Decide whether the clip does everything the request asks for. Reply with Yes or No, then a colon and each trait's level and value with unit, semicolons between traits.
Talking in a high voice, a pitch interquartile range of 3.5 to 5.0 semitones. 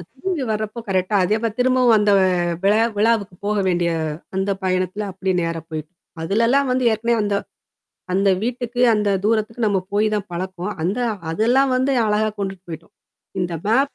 Yes: high, 210 Hz; average, 3.8 semitones